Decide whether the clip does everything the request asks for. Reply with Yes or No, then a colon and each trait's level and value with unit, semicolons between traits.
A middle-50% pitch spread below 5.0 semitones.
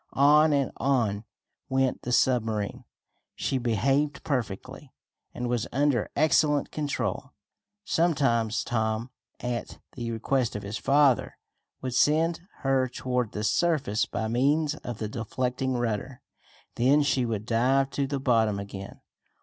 Yes: average, 3.6 semitones